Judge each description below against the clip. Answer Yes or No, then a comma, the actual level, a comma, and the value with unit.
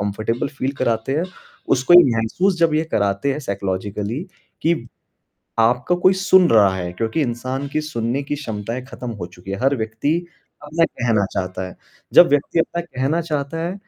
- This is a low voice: Yes, low, 130 Hz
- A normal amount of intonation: No, wide, 6.2 semitones